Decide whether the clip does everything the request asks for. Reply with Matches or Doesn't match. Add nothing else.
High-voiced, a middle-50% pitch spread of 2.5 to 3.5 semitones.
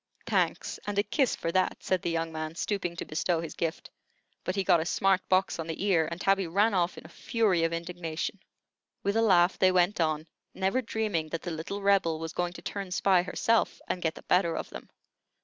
Doesn't match